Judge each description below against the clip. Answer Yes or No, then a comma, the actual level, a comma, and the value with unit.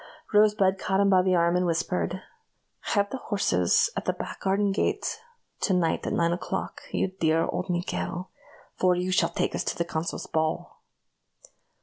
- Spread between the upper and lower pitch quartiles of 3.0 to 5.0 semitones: No, narrow, 2.4 semitones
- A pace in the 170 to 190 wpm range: Yes, average, 175 wpm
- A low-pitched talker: No, medium, 180 Hz